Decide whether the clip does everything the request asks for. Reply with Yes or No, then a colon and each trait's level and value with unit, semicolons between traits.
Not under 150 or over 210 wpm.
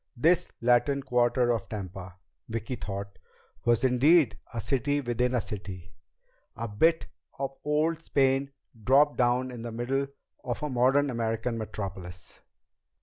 No: slow, 135 wpm